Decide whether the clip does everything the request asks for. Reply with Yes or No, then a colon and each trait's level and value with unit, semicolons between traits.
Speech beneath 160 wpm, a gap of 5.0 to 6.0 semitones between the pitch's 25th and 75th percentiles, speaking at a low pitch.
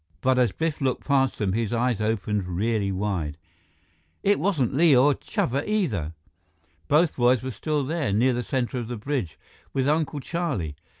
No: average, 170 wpm; wide, 5.6 semitones; low, 125 Hz